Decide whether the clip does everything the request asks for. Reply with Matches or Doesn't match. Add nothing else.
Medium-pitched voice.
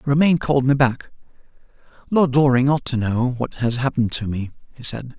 Doesn't match